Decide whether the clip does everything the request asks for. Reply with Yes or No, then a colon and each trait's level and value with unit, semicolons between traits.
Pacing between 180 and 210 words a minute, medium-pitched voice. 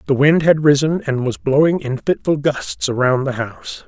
Yes: average, 200 wpm; medium, 145 Hz